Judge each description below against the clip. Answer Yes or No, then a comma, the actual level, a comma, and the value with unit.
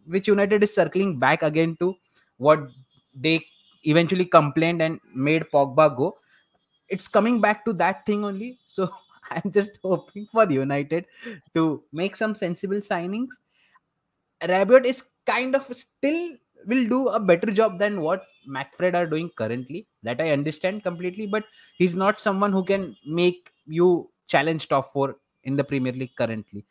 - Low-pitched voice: No, medium, 180 Hz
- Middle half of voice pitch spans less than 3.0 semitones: No, average, 5.1 semitones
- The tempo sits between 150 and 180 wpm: Yes, average, 155 wpm